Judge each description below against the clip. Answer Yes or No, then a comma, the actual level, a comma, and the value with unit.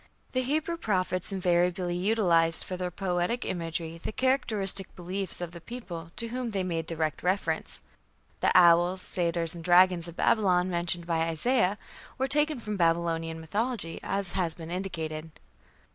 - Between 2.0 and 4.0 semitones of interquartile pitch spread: Yes, average, 3.3 semitones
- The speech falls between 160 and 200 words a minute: No, average, 150 wpm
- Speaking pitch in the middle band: Yes, medium, 180 Hz